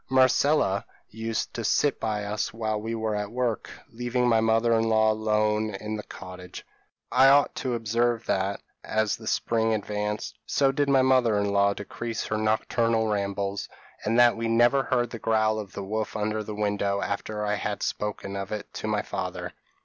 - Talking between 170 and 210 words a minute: Yes, average, 190 wpm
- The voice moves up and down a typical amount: No, narrow, 2.0 semitones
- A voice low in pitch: Yes, low, 110 Hz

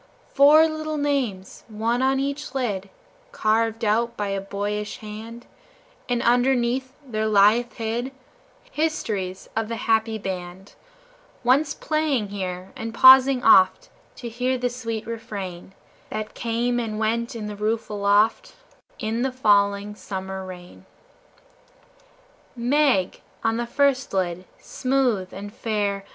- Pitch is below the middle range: No, high, 225 Hz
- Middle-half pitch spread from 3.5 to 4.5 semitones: Yes, average, 3.8 semitones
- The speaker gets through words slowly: Yes, slow, 125 wpm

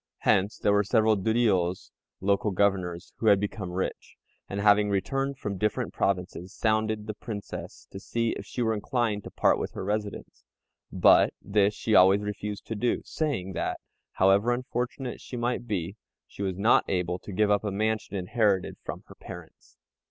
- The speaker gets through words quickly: No, average, 175 wpm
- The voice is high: No, low, 105 Hz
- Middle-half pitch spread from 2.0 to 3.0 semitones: Yes, narrow, 2.4 semitones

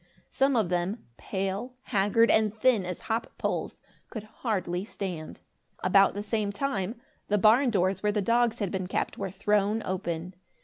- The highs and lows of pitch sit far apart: No, average, 3.0 semitones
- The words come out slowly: No, average, 165 wpm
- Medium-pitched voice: No, high, 205 Hz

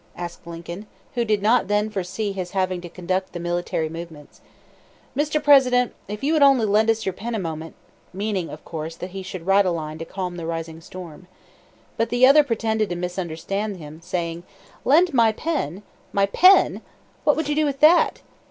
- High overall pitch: Yes, high, 195 Hz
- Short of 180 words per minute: No, average, 195 wpm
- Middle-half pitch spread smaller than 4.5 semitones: No, average, 5.1 semitones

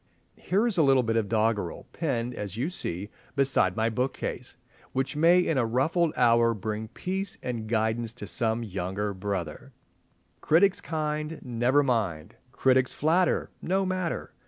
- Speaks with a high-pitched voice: No, low, 120 Hz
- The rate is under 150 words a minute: Yes, average, 140 wpm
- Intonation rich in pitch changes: Yes, wide, 6.1 semitones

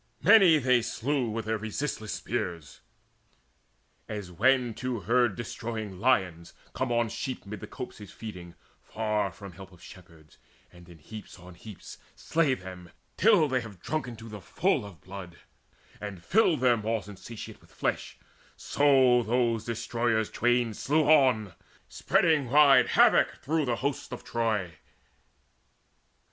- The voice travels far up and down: No, average, 4.7 semitones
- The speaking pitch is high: No, low, 115 Hz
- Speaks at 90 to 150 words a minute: Yes, average, 140 wpm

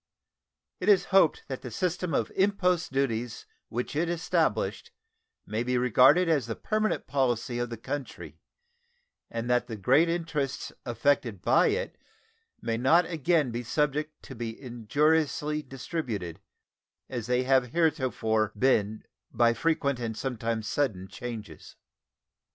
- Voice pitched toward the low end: Yes, low, 130 Hz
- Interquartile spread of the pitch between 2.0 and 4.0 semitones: No, average, 5.2 semitones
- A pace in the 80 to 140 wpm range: Yes, slow, 135 wpm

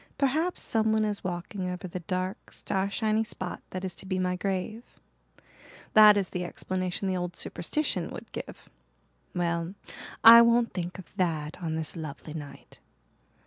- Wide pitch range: No, average, 3.4 semitones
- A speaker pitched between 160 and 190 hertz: Yes, medium, 185 Hz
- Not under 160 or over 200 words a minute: No, average, 150 wpm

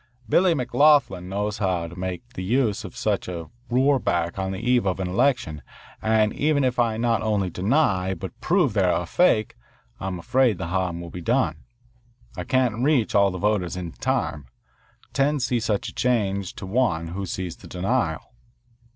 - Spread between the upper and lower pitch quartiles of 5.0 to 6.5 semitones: Yes, average, 5.3 semitones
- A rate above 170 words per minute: Yes, average, 185 wpm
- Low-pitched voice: Yes, low, 100 Hz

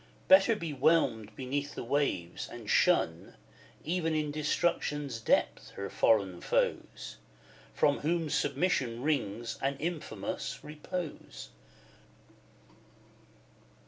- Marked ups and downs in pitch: Yes, wide, 5.8 semitones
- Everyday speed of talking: No, slow, 95 wpm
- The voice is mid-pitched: Yes, medium, 145 Hz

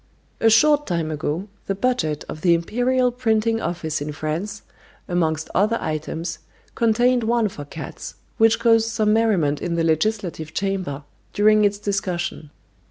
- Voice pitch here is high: Yes, high, 195 Hz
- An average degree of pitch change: No, wide, 5.9 semitones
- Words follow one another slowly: No, average, 145 wpm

